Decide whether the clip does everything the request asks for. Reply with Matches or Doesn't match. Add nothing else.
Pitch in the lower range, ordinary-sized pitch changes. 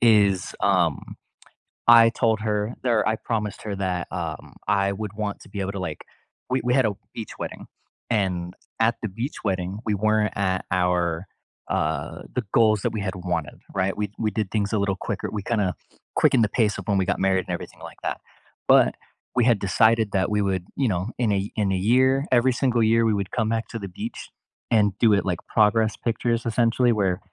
Matches